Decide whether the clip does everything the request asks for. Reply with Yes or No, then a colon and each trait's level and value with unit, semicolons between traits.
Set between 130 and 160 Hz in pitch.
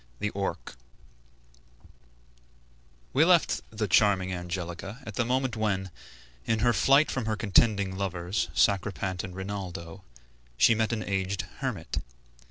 No: low, 100 Hz